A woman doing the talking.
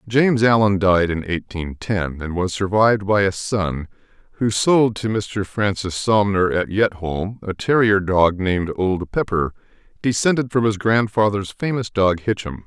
No: male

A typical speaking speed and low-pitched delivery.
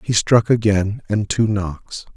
Yes: average, 165 wpm; low, 105 Hz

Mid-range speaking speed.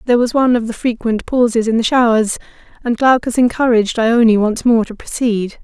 Yes: average, 190 wpm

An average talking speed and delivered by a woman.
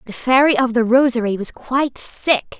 Yes: average, 185 wpm; female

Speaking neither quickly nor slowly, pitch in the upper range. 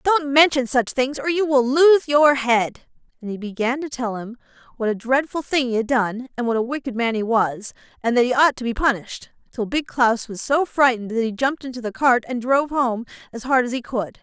No: fast, 240 wpm; very high, 250 Hz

